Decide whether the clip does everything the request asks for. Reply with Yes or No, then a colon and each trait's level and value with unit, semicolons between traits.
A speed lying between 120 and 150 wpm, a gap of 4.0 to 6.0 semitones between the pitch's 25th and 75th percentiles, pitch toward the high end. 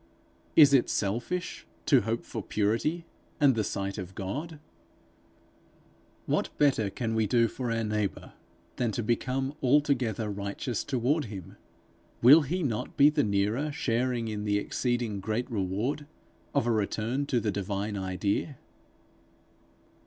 No: average, 140 wpm; average, 4.6 semitones; low, 115 Hz